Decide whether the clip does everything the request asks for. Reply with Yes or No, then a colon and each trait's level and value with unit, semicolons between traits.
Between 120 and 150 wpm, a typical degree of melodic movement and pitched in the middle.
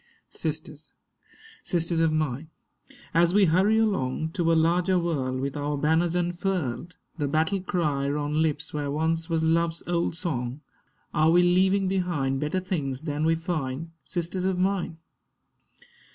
Yes: average, 145 wpm; average, 3.1 semitones; medium, 165 Hz